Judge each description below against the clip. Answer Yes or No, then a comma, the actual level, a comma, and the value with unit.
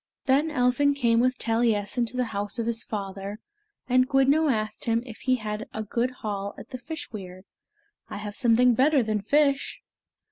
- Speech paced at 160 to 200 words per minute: Yes, average, 180 wpm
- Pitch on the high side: Yes, high, 235 Hz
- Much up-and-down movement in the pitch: No, average, 3.5 semitones